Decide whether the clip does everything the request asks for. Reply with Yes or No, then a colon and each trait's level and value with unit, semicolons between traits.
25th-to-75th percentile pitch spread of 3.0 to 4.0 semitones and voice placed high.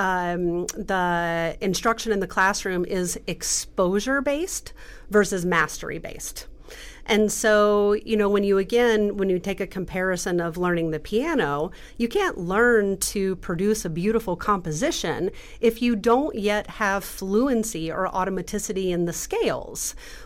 Yes: average, 3.3 semitones; high, 195 Hz